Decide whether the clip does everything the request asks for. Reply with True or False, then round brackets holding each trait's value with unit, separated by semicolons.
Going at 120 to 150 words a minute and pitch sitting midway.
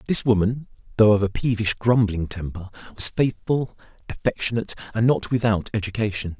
False (140 wpm; 110 Hz)